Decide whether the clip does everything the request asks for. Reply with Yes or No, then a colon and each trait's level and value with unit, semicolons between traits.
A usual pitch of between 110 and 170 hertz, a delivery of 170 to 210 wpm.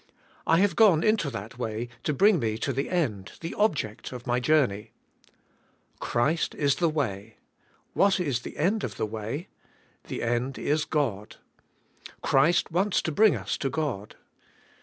No: medium, 140 Hz; average, 160 wpm